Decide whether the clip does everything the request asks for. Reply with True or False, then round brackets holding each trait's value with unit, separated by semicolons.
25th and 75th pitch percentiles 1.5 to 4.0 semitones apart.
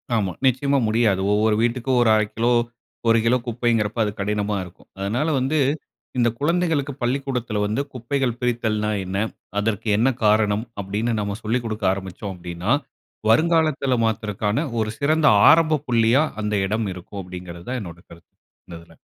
True (3.6 semitones)